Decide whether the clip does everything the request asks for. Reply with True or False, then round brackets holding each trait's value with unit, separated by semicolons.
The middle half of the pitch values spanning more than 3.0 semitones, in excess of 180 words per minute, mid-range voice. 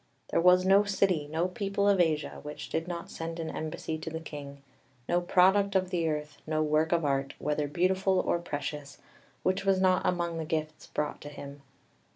True (3.5 semitones; 195 wpm; 165 Hz)